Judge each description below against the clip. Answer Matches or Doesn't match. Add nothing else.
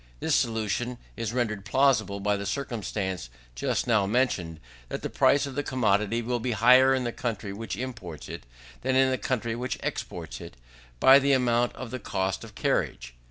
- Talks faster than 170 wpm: Matches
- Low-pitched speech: Matches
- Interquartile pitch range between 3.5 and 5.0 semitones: Matches